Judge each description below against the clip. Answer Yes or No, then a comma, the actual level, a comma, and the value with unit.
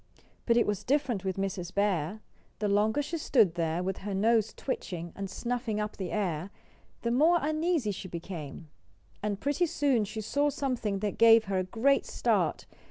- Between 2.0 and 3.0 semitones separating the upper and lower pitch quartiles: No, average, 4.6 semitones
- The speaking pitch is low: No, high, 210 Hz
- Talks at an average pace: Yes, average, 175 wpm